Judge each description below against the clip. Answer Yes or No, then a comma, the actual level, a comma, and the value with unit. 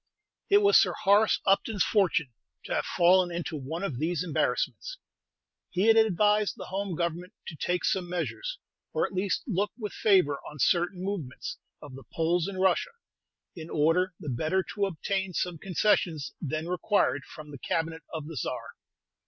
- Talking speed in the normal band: Yes, average, 170 wpm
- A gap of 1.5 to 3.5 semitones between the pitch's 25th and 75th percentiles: No, average, 3.9 semitones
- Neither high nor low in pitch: Yes, medium, 180 Hz